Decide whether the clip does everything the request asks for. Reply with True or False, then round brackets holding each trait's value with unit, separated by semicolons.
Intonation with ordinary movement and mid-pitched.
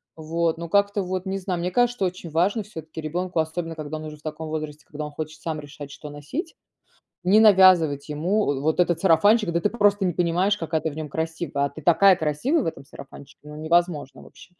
True (3.5 semitones; 165 Hz)